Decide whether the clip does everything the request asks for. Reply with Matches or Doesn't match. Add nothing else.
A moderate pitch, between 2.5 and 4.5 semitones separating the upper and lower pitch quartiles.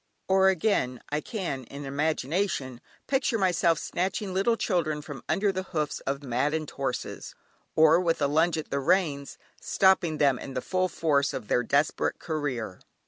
Doesn't match